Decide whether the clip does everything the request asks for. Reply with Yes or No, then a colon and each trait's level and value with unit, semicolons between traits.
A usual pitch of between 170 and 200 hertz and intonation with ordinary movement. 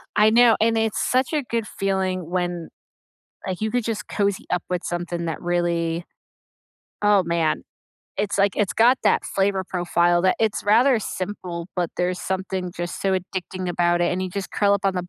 Yes: medium, 185 Hz; average, 3.0 semitones